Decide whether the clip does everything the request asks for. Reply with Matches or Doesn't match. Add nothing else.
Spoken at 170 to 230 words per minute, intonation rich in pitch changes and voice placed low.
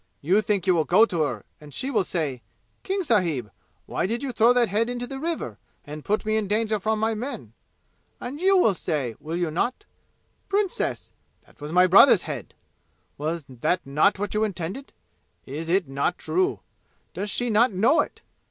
Doesn't match